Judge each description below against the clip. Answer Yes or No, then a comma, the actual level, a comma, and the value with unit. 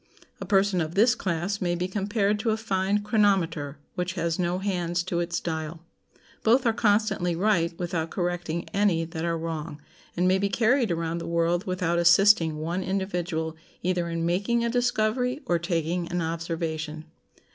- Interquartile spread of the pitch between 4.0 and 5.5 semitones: No, average, 3.2 semitones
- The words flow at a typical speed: Yes, average, 170 wpm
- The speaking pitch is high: No, medium, 175 Hz